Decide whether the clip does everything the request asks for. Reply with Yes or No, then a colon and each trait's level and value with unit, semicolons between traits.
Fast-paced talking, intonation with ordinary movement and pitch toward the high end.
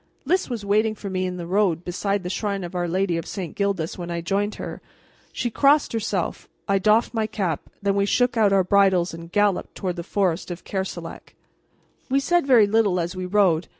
Yes: fast, 210 wpm; average, 3.0 semitones; high, 195 Hz